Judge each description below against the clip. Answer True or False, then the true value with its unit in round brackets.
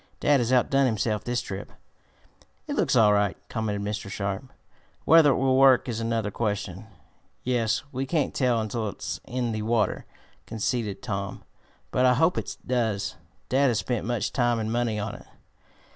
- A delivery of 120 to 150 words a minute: False (170 wpm)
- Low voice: True (115 Hz)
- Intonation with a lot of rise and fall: False (3.4 semitones)